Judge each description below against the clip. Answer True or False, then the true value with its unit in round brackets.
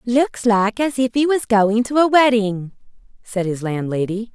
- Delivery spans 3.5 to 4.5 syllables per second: True (4.3 syllables/s)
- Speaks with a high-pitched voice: True (225 Hz)